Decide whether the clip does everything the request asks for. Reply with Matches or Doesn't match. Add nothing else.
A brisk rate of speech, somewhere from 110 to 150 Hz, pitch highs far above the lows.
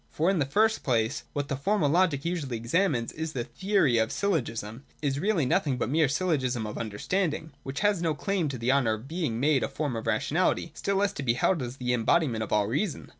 Matches